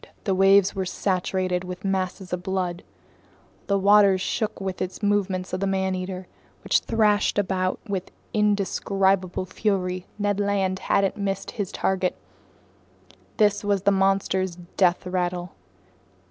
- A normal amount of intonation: No, narrow, 1.5 semitones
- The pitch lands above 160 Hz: Yes, high, 190 Hz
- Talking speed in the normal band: No, slow, 130 wpm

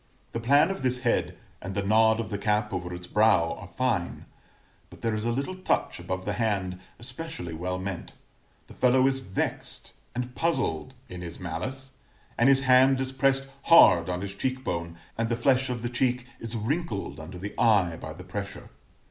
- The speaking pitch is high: No, low, 115 Hz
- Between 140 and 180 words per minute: No, average, 190 wpm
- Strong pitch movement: Yes, wide, 6.0 semitones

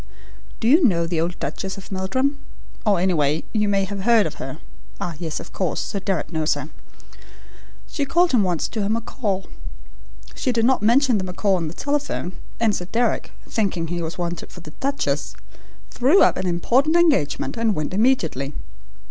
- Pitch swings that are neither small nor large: No, wide, 5.8 semitones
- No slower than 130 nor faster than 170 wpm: No, average, 185 wpm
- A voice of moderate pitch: No, high, 195 Hz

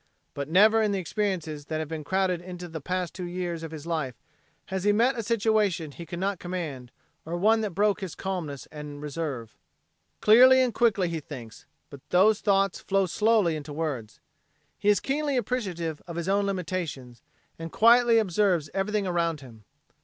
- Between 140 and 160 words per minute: No, average, 185 wpm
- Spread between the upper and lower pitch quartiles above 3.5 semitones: Yes, average, 4.7 semitones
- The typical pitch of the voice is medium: Yes, medium, 180 Hz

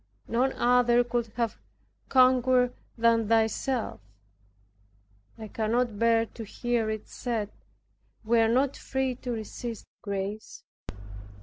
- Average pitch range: No, narrow, 2.0 semitones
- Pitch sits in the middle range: No, high, 235 Hz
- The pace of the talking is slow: Yes, slow, 110 wpm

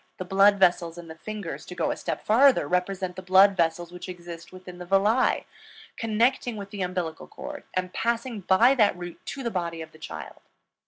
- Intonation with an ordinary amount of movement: Yes, average, 3.4 semitones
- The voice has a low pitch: No, medium, 185 Hz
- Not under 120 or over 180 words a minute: No, average, 200 wpm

